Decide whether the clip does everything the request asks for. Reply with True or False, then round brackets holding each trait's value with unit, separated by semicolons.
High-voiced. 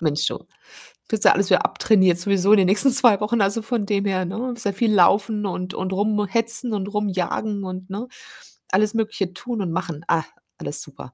True (200 Hz)